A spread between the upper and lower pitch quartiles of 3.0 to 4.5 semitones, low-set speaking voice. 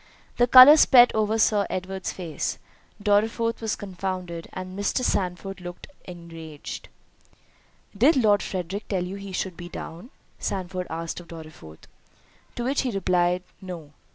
No: average, 3.5 semitones; medium, 185 Hz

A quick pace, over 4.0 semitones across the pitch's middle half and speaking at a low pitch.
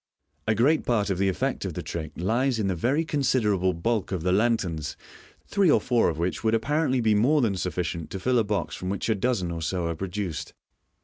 Yes: fast, 235 wpm; average, 5.1 semitones; low, 105 Hz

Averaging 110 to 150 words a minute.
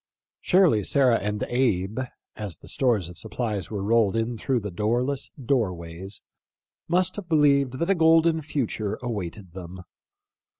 Yes: average, 145 wpm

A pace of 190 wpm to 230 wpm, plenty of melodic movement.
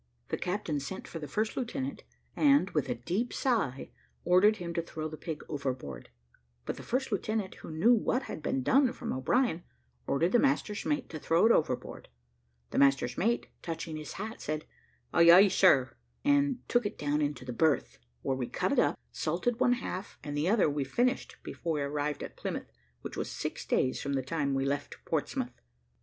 Yes: average, 195 wpm; wide, 7.8 semitones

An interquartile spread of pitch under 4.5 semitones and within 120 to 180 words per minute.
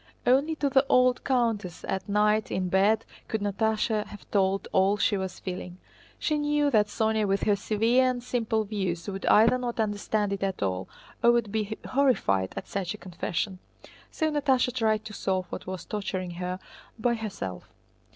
Yes: average, 3.8 semitones; average, 175 wpm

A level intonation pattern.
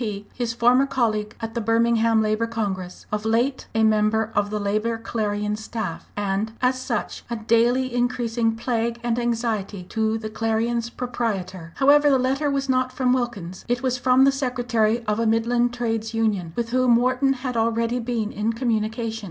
Yes: narrow, 2.2 semitones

